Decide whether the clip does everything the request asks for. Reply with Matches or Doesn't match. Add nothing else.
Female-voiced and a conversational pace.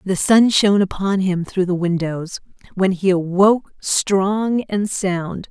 Matches